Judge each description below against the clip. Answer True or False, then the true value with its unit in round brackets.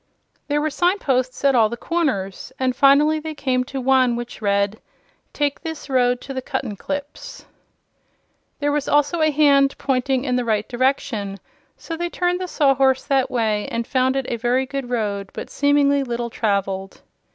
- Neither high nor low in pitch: False (265 Hz)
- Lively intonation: False (3.4 semitones)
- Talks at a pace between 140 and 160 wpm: False (170 wpm)